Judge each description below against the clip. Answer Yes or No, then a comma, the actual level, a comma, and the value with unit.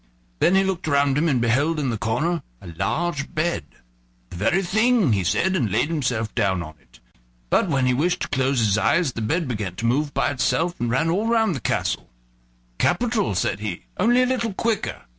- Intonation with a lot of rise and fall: Yes, wide, 7.7 semitones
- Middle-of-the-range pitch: Yes, medium, 145 Hz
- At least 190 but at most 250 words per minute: Yes, fast, 205 wpm